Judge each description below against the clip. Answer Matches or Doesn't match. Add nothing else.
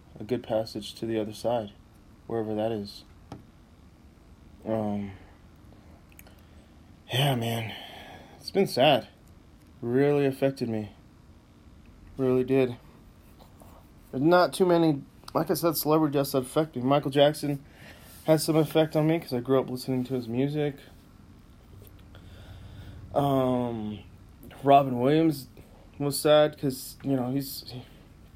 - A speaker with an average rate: Doesn't match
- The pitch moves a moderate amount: Doesn't match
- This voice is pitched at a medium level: Doesn't match